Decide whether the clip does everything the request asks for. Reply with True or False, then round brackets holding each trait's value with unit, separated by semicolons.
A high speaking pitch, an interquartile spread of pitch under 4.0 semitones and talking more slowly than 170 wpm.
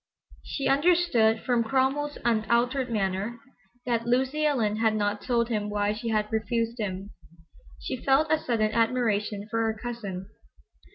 True (230 Hz; 3.1 semitones; 145 wpm)